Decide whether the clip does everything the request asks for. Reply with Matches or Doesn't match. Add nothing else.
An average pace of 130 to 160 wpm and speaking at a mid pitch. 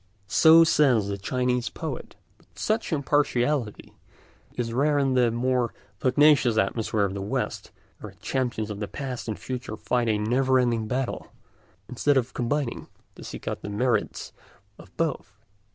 Doesn't match